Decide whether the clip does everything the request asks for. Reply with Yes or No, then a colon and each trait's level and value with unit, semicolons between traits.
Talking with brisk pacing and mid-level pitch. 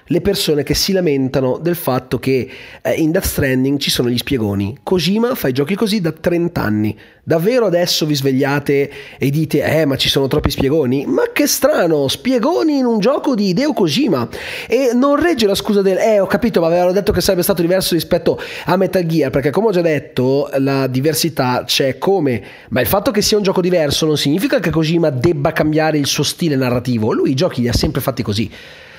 Yes: fast, 205 wpm; medium, 160 Hz